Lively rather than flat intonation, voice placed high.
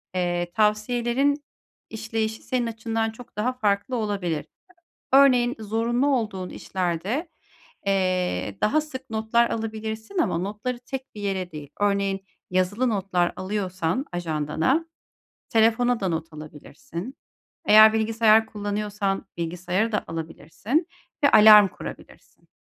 No: average, 4.2 semitones; high, 215 Hz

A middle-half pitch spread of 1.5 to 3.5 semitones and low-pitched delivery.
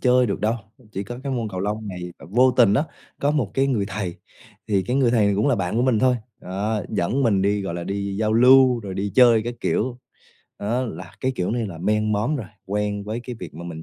No: average, 3.9 semitones; low, 110 Hz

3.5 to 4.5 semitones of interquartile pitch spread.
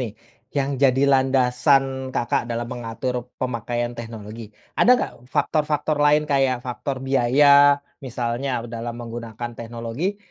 No: average, 2.7 semitones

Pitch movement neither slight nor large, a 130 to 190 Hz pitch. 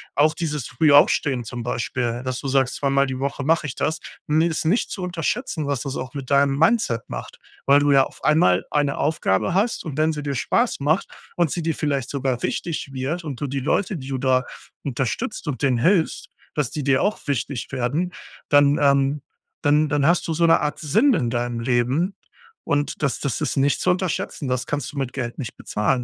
Yes: average, 3.3 semitones; medium, 140 Hz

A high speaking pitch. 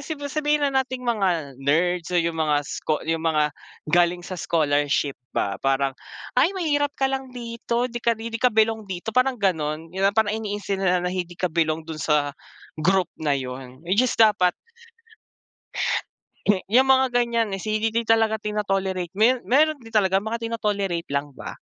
Yes: high, 195 Hz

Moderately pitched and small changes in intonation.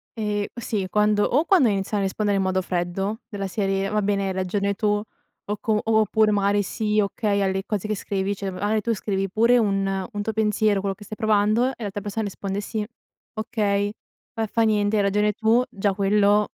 No: high, 205 Hz; narrow, 1.6 semitones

